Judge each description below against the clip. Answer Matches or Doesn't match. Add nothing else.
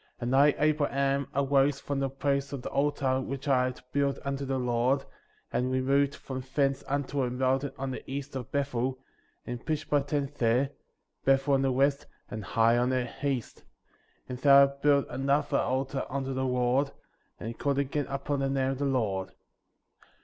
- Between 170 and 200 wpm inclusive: Matches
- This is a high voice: Doesn't match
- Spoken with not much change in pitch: Matches